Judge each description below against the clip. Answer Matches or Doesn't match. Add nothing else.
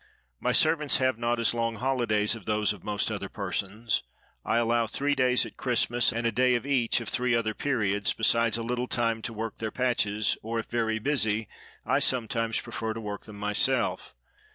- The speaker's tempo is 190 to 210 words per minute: Matches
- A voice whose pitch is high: Doesn't match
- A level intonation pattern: Matches